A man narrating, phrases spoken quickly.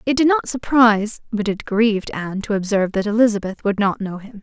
No: female; fast, 215 wpm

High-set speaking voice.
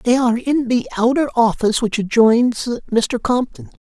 Yes: high, 235 Hz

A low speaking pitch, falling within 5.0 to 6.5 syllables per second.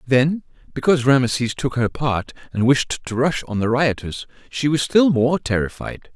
No: low, 130 Hz; 4.7 syllables/s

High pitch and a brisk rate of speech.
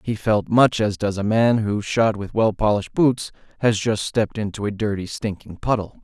No: low, 105 Hz; fast, 210 wpm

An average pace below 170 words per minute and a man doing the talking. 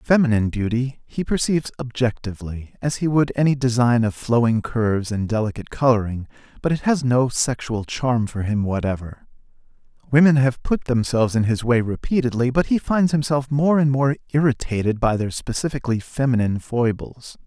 Yes: average, 160 wpm; male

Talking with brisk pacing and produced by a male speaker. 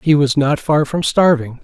Yes: fast, 220 wpm; male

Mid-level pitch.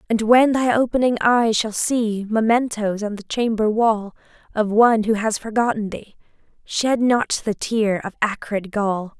No: high, 220 Hz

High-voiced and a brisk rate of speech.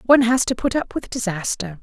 Yes: high, 225 Hz; fast, 230 wpm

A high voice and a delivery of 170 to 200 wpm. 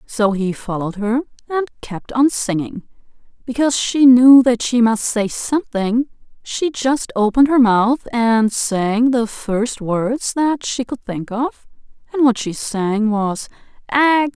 No: high, 235 Hz; average, 155 wpm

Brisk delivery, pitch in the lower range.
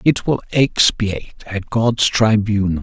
No: slow, 125 wpm; low, 110 Hz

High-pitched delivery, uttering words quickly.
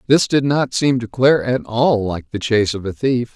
No: low, 120 Hz; fast, 250 wpm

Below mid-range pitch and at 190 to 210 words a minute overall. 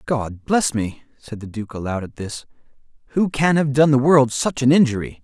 Yes: low, 130 Hz; fast, 205 wpm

